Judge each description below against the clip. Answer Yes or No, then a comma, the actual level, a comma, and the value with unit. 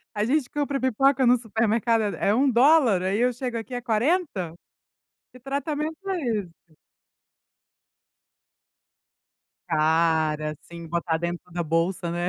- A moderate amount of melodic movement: No, wide, 7.4 semitones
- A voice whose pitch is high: Yes, high, 225 Hz